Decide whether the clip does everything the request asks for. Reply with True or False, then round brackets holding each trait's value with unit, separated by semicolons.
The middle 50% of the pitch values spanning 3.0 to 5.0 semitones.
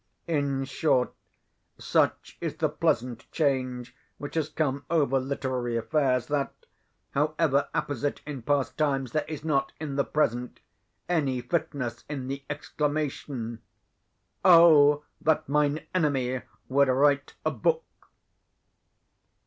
False (2.6 semitones)